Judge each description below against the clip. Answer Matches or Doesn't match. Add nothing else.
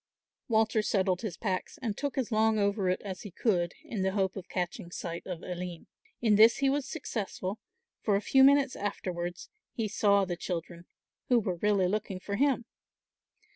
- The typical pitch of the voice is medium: Doesn't match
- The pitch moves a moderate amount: Matches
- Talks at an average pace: Matches